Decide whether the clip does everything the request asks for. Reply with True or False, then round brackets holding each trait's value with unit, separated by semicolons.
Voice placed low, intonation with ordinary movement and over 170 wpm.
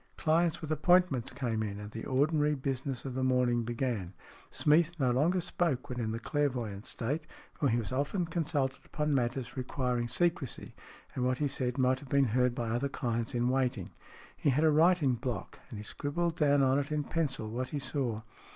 True (130 Hz; 3.6 semitones; 190 wpm)